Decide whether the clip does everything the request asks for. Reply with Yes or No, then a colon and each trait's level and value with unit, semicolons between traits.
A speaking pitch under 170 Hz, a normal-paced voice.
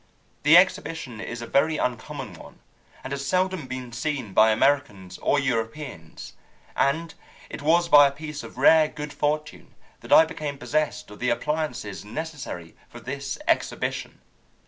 Yes: medium, 140 Hz; average, 150 wpm